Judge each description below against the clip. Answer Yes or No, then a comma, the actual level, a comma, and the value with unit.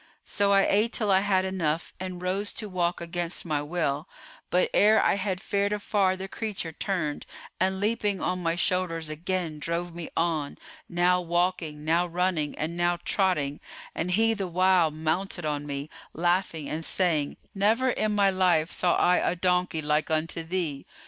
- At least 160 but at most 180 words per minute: Yes, average, 170 wpm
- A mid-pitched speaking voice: Yes, medium, 180 Hz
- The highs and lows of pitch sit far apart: No, average, 2.8 semitones